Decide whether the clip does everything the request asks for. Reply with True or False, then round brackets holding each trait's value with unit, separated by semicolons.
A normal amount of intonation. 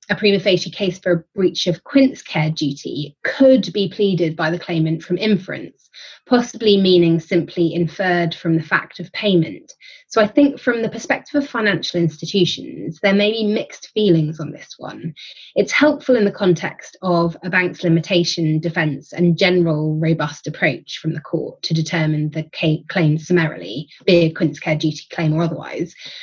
True (3.8 semitones)